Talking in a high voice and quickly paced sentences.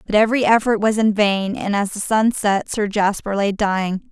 Yes: high, 205 Hz; fast, 220 wpm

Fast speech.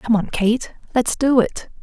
No: average, 195 wpm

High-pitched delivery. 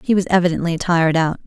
No: medium, 170 Hz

